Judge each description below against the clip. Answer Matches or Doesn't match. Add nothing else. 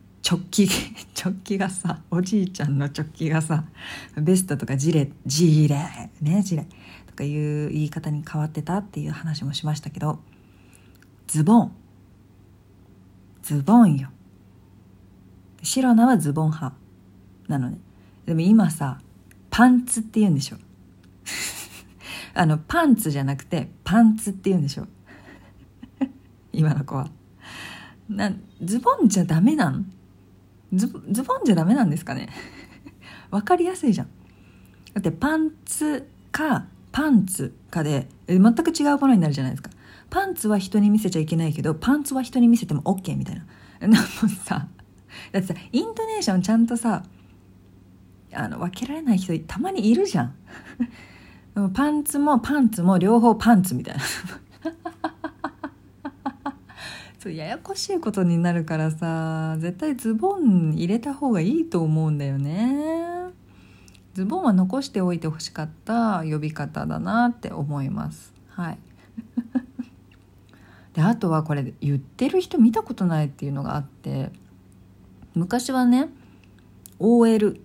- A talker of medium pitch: Matches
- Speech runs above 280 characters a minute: Doesn't match